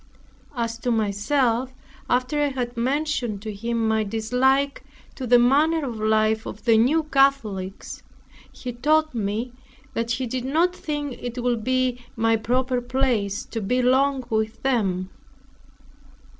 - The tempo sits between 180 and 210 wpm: No, average, 145 wpm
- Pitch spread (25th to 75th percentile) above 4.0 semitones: No, average, 3.2 semitones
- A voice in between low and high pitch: No, high, 245 Hz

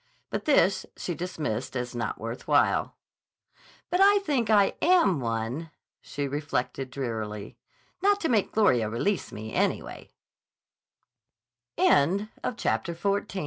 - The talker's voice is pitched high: No, medium, 145 Hz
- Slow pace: Yes, slow, 105 wpm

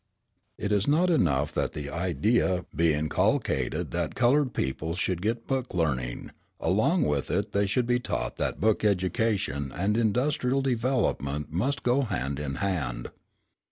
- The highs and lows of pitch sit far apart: Yes, wide, 8.4 semitones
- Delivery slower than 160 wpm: Yes, average, 150 wpm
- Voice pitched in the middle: No, low, 100 Hz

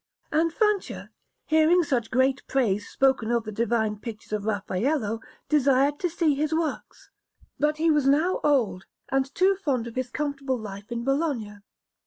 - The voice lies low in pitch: No, very high, 270 Hz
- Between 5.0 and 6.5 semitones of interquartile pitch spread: Yes, average, 5.3 semitones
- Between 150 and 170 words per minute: Yes, average, 160 wpm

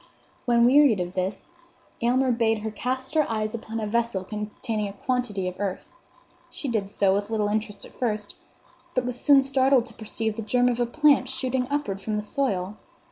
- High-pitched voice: Yes, high, 225 Hz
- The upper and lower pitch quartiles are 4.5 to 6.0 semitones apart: No, average, 3.5 semitones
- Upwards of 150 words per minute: Yes, average, 190 wpm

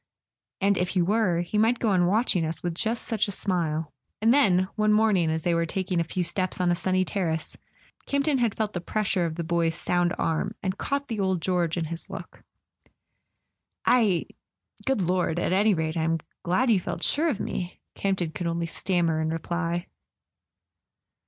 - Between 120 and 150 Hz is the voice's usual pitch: No, medium, 180 Hz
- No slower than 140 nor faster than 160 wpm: No, average, 190 wpm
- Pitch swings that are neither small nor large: Yes, average, 3.7 semitones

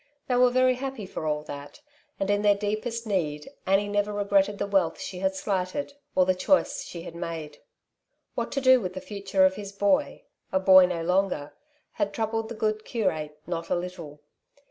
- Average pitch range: Yes, average, 3.3 semitones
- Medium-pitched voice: No, high, 195 Hz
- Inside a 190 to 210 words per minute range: Yes, average, 200 wpm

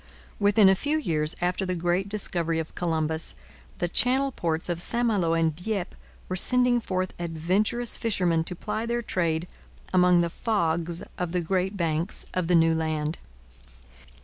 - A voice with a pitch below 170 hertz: No, medium, 180 Hz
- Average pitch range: Yes, average, 3.7 semitones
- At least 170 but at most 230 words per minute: No, average, 160 wpm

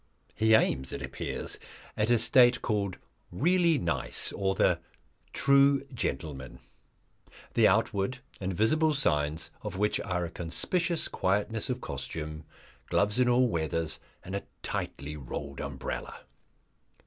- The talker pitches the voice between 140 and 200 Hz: No, low, 100 Hz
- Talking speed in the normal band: No, slow, 125 wpm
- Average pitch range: No, wide, 7.4 semitones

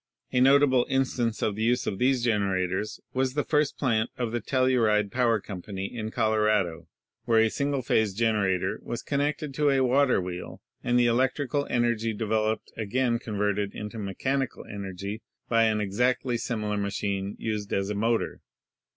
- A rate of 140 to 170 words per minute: Yes, average, 160 wpm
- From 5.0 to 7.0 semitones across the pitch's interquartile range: No, average, 3.6 semitones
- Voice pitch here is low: Yes, low, 115 Hz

